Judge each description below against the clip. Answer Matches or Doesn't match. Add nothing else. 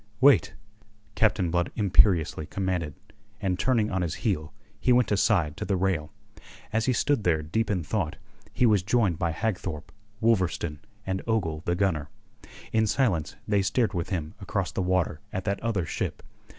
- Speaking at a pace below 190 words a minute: Matches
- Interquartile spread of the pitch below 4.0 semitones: Doesn't match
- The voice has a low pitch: Matches